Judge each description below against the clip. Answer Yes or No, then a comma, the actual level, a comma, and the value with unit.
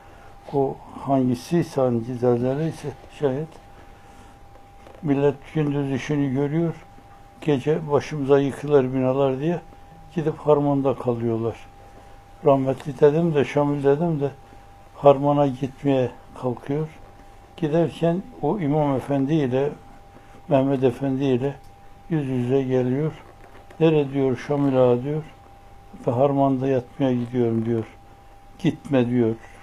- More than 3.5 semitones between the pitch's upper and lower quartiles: Yes, average, 4.1 semitones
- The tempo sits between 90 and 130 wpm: Yes, average, 100 wpm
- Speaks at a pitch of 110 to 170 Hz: Yes, low, 135 Hz